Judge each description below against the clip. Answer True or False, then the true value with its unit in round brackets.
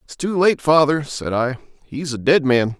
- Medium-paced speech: False (215 wpm)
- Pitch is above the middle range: False (140 Hz)